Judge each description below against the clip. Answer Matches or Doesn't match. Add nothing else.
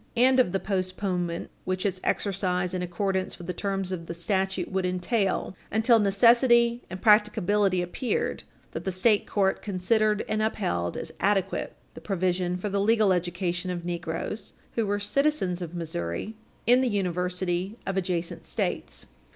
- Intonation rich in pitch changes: Doesn't match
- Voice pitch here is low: Doesn't match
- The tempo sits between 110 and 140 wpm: Doesn't match